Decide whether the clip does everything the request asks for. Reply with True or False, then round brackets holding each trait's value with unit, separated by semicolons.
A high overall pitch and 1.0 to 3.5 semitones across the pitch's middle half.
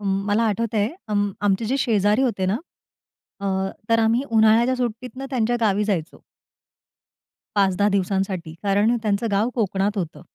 True (210 Hz; 2.5 semitones)